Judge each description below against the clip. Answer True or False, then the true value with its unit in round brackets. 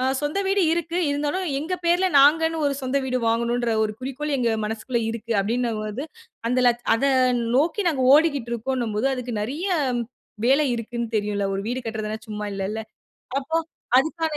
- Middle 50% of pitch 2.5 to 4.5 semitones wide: False (4.9 semitones)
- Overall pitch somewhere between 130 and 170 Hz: False (255 Hz)